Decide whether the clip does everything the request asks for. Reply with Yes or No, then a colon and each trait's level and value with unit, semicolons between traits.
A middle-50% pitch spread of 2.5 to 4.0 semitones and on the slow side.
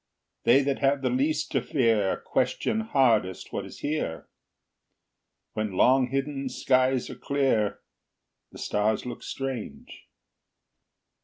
Yes: average, 3.4 semitones; slow, 115 wpm